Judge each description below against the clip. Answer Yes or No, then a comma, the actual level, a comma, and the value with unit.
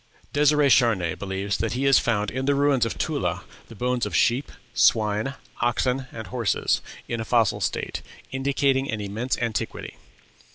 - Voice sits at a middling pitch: No, low, 120 Hz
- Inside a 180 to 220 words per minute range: No, average, 160 wpm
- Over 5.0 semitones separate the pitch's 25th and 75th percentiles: No, average, 3.4 semitones